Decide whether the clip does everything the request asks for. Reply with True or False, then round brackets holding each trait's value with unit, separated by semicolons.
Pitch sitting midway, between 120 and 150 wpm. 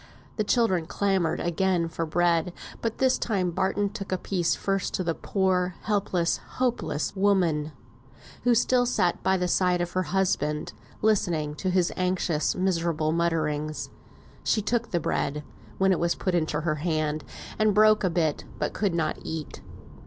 False (180 Hz; 160 wpm)